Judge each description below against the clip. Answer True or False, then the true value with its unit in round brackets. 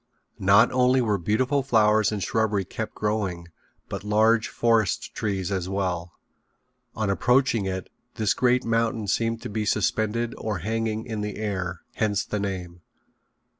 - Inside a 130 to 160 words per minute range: True (145 wpm)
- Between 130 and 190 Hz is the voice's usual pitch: False (105 Hz)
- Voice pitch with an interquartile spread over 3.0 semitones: False (2.7 semitones)